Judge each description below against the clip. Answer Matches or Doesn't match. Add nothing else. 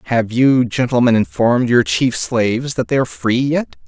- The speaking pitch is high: Doesn't match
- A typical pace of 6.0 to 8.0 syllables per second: Doesn't match